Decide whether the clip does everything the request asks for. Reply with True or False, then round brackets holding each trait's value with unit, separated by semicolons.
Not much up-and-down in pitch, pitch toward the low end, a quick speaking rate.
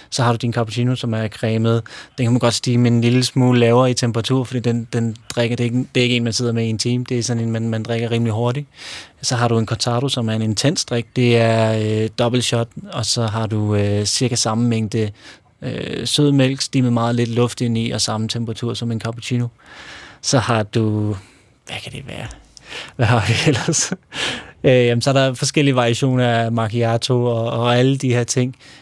True (1.5 semitones; 120 Hz; 230 wpm)